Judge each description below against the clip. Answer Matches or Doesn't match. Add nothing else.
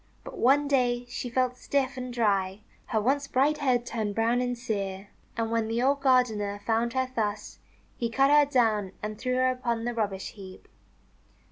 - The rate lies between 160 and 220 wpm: Matches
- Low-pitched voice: Doesn't match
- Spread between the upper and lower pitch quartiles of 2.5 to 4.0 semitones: Matches